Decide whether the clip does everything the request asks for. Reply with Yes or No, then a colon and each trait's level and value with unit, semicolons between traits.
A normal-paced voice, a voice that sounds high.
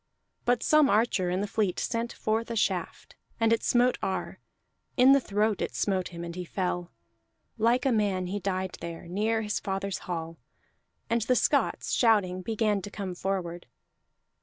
Yes: average, 170 wpm; high, 205 Hz